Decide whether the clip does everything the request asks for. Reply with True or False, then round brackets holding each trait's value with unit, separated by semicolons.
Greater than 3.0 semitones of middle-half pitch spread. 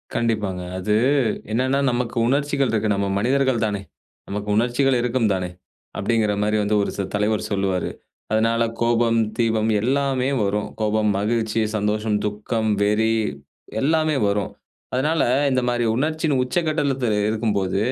True (3.7 semitones)